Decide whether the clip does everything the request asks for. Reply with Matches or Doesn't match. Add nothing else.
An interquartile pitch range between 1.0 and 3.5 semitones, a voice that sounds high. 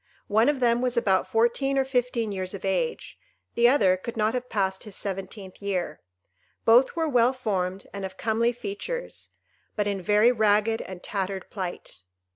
Doesn't match